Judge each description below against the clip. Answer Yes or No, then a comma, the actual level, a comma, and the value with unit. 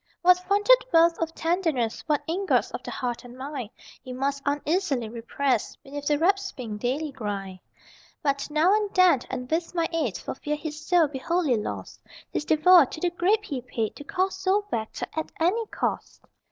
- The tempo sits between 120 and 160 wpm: No, average, 180 wpm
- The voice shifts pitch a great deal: Yes, wide, 5.7 semitones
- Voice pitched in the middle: No, very high, 305 Hz